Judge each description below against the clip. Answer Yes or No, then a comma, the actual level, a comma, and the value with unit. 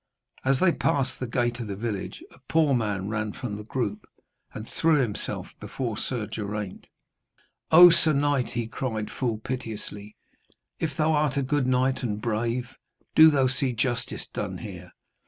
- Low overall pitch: Yes, low, 125 Hz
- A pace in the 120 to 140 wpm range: No, average, 170 wpm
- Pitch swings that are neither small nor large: Yes, average, 4.3 semitones